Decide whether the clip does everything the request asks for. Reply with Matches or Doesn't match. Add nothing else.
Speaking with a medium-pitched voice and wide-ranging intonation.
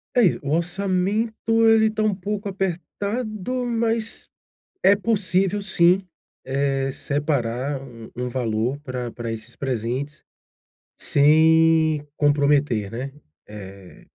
Matches